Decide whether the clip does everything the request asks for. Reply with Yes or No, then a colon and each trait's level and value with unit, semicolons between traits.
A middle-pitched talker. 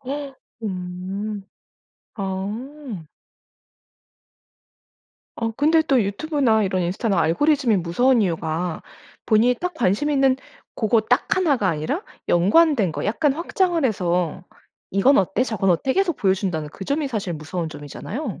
No: high, 220 Hz